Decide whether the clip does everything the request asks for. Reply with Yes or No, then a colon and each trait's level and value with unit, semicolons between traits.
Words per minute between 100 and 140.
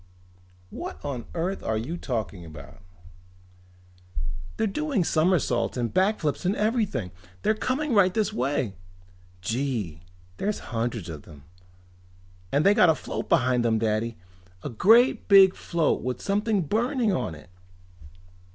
Yes: slow, 135 wpm